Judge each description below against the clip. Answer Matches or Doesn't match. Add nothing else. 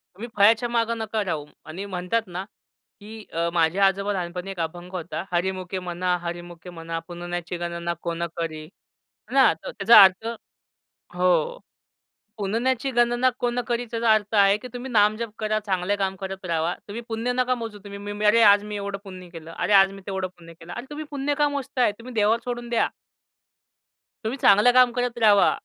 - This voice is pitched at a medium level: Doesn't match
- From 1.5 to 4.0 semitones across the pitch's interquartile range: Doesn't match